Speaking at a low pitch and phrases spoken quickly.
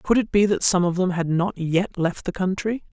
No: medium, 185 Hz; fast, 260 wpm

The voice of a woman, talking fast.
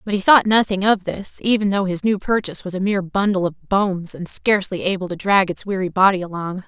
Yes: female; fast, 235 wpm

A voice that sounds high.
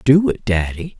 No: low, 125 Hz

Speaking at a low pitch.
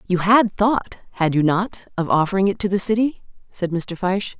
No: high, 195 Hz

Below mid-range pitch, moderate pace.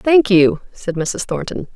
No: high, 200 Hz; average, 170 wpm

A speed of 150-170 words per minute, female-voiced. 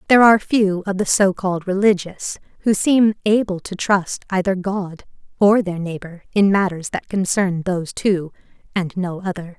Yes: average, 165 wpm; female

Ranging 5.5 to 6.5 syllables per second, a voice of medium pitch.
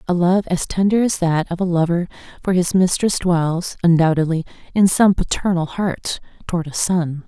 No: 4.9 syllables/s; medium, 175 Hz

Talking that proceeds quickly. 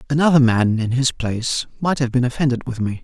Yes: fast, 220 wpm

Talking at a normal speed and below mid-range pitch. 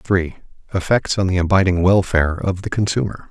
Yes: average, 165 wpm; very low, 95 Hz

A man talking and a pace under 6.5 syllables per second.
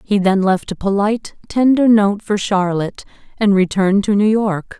No: female; 5.0 syllables/s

